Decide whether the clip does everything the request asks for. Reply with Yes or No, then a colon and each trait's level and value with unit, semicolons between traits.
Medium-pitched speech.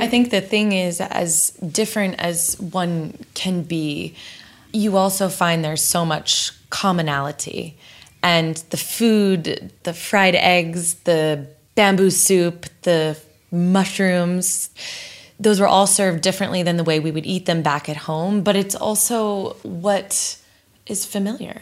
Yes: medium, 180 Hz